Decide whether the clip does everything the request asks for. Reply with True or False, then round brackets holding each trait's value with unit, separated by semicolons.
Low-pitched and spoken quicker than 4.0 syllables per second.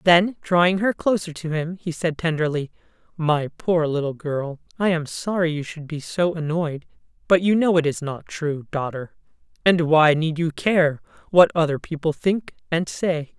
False (165 Hz; 4.5 syllables/s)